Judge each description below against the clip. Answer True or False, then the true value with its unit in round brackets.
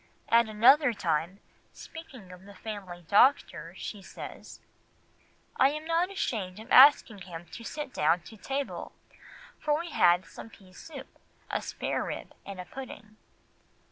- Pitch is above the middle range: True (215 Hz)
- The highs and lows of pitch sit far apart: True (6.9 semitones)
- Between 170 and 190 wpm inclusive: False (140 wpm)